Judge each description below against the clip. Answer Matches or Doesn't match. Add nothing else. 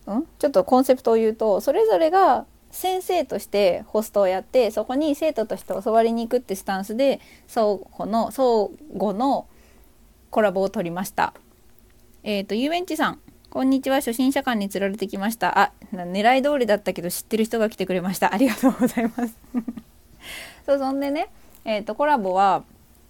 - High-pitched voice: Matches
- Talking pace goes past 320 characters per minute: Matches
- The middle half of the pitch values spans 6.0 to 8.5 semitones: Doesn't match